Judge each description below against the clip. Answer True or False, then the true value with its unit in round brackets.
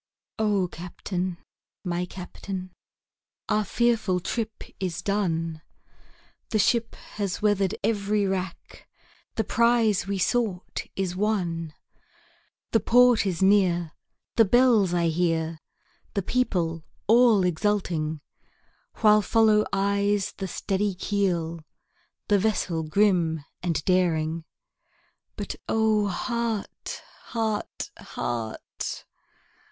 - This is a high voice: True (195 Hz)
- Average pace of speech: False (100 wpm)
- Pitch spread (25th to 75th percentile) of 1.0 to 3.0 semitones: False (3.5 semitones)